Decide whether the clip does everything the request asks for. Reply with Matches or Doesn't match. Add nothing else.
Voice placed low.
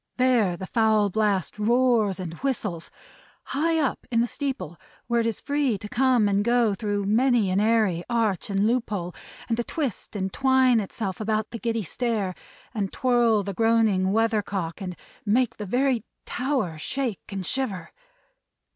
Doesn't match